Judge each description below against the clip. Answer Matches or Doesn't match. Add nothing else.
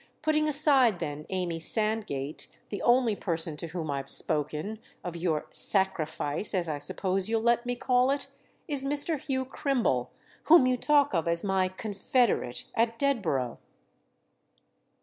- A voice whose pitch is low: Doesn't match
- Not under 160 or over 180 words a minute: Doesn't match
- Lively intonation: Matches